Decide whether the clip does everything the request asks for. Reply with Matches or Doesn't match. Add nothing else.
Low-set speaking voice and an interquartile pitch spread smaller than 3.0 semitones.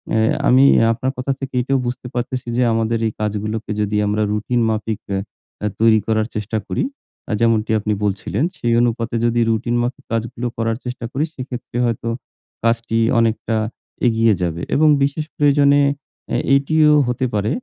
Matches